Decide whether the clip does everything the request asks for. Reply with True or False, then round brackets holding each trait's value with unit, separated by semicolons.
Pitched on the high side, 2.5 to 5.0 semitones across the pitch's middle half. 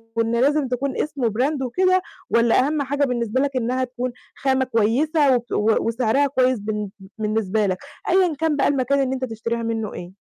True (255 Hz; 3.5 semitones)